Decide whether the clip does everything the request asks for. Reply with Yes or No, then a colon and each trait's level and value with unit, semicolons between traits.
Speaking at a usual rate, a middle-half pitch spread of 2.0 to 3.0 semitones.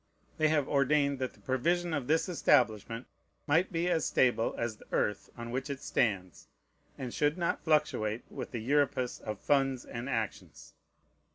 No: average, 165 wpm; average, 4.3 semitones